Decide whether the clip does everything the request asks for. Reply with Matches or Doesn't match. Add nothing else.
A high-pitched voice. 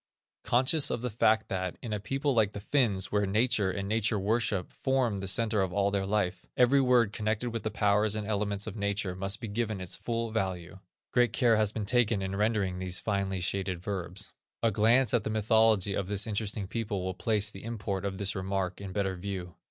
Doesn't match